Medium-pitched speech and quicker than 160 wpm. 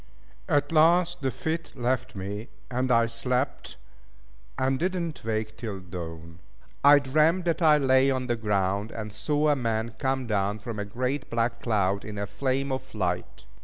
No: low, 125 Hz; average, 170 wpm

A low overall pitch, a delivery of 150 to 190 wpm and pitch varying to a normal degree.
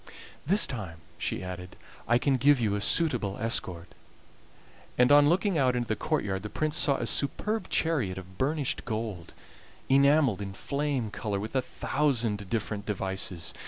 No: low, 115 Hz; average, 160 wpm; wide, 6.2 semitones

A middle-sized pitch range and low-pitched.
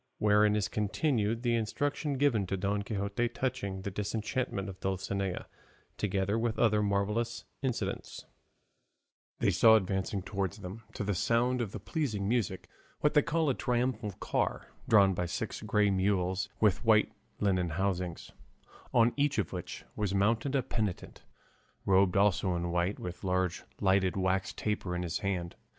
Yes: average, 3.4 semitones; low, 100 Hz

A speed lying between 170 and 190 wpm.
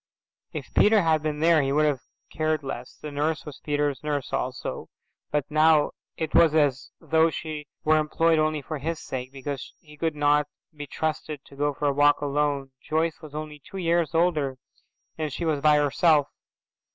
Yes: average, 185 wpm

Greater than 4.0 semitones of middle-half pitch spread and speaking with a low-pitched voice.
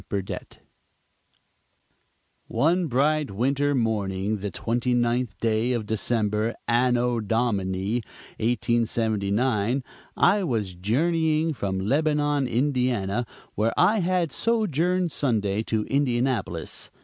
Yes: average, 5.2 semitones; low, 120 Hz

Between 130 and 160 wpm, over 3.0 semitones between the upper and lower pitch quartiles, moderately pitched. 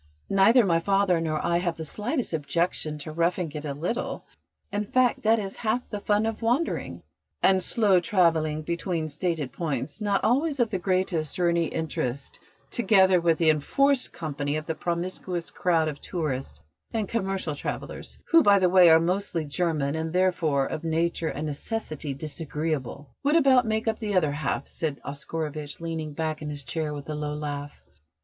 No: average, 175 wpm; average, 4.5 semitones; medium, 165 Hz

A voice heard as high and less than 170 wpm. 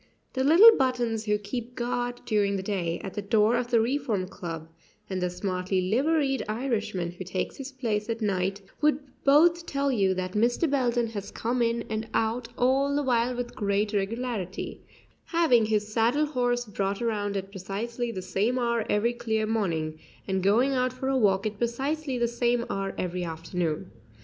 No: high, 225 Hz; average, 180 wpm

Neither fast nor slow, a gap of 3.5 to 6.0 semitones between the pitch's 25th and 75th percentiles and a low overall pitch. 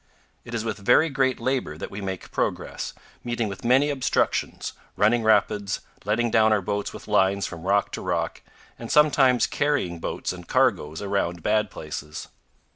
Yes: average, 165 wpm; average, 4.1 semitones; low, 105 Hz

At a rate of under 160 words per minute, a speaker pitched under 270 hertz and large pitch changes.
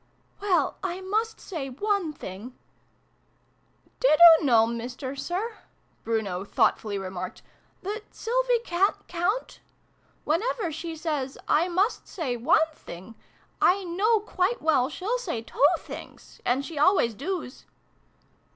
No: average, 140 wpm; very high, 330 Hz; wide, 8.1 semitones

